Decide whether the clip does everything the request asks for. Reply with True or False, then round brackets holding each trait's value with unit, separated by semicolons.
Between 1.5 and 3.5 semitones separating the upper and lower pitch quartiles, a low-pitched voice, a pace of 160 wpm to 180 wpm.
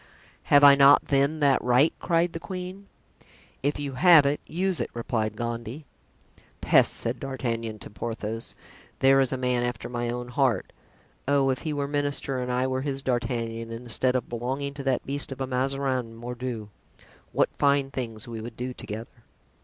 True (2.9 semitones; 130 Hz; 175 wpm)